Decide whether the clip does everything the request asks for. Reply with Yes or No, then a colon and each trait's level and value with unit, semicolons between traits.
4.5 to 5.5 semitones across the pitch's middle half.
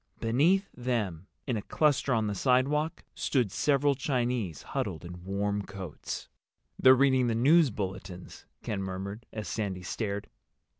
Yes: average, 5.2 semitones